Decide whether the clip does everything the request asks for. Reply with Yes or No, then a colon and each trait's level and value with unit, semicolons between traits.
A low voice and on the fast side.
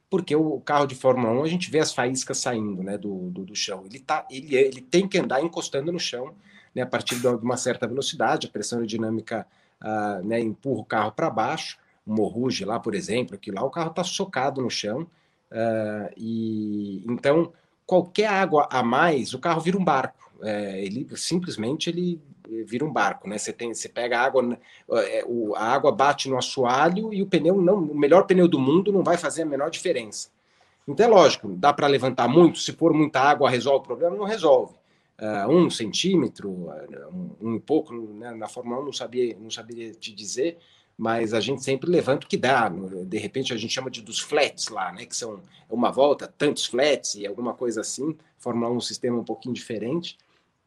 Yes: low, 130 Hz; fast, 200 wpm